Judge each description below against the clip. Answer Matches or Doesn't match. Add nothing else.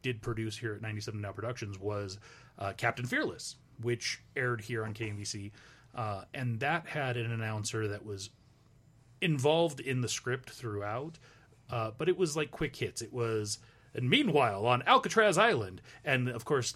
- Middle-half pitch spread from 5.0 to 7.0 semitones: Doesn't match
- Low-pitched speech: Matches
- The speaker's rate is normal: Matches